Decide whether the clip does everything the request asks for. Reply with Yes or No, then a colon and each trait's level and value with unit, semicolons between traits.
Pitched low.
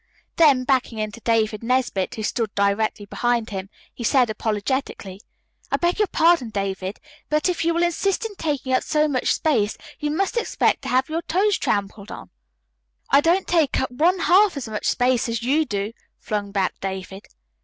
No: very high, 250 Hz